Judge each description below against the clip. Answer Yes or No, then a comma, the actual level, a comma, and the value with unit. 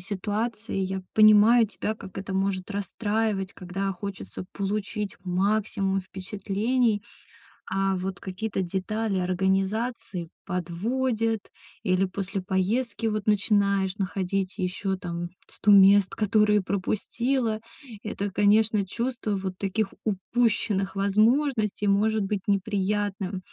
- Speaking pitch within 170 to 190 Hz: No, high, 200 Hz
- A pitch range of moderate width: No, narrow, 2.2 semitones